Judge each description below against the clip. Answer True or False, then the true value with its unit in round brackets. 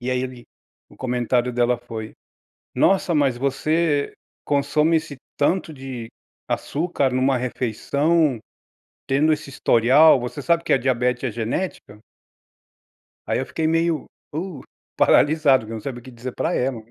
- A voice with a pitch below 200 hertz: True (135 Hz)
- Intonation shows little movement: False (4.0 semitones)